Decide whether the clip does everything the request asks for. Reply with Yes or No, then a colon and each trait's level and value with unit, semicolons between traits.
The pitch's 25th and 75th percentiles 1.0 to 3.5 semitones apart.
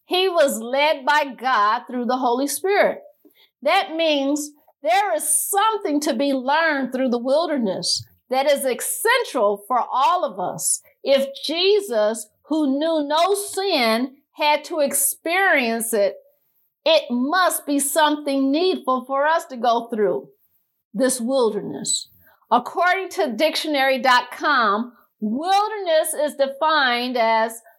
No: average, 4.5 semitones